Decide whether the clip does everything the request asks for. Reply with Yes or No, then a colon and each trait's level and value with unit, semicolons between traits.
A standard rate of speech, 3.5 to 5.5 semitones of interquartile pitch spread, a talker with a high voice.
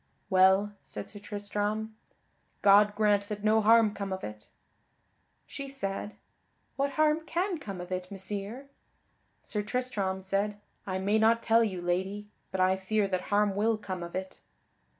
No: average, 155 wpm; narrow, 2.5 semitones; high, 205 Hz